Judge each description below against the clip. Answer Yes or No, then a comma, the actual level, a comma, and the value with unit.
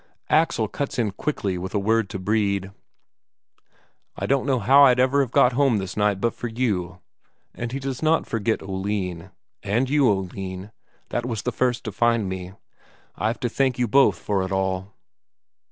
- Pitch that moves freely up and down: No, average, 4.7 semitones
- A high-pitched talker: No, low, 110 Hz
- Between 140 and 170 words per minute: No, average, 180 wpm